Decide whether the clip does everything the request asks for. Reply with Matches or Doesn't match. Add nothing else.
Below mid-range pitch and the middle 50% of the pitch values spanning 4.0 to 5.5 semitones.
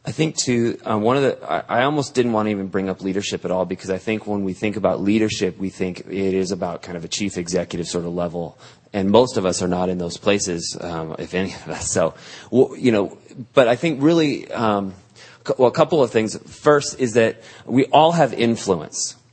Matches